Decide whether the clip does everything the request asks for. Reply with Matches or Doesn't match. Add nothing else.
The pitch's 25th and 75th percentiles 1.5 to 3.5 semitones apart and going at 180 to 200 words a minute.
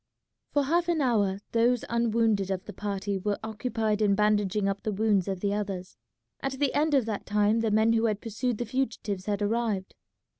Matches